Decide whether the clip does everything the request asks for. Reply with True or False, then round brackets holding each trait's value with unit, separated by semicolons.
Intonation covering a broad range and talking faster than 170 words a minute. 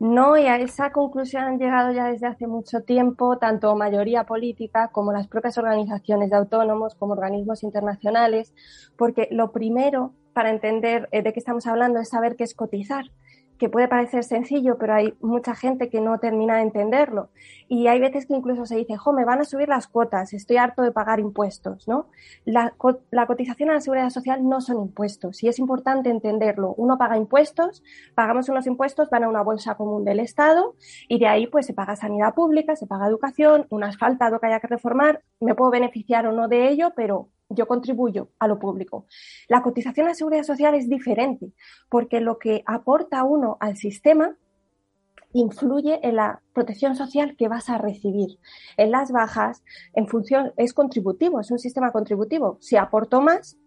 False (3.1 semitones; 185 wpm)